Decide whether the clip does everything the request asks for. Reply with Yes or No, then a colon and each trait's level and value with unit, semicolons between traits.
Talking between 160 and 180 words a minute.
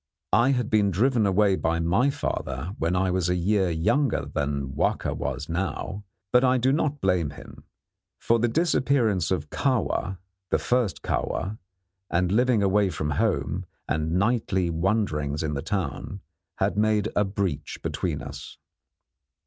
No: average, 150 wpm